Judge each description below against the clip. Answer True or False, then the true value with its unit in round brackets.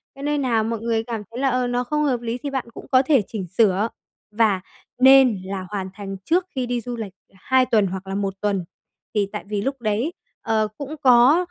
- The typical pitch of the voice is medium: False (230 Hz)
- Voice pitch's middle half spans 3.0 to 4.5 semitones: True (4.1 semitones)